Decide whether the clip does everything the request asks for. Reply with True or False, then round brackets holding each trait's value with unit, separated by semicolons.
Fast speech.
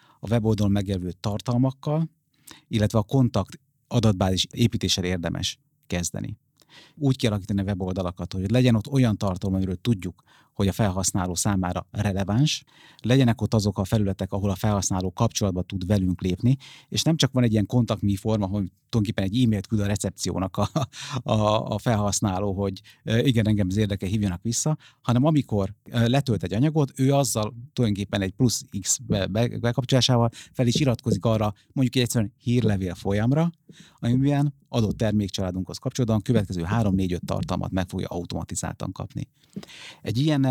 False (145 wpm)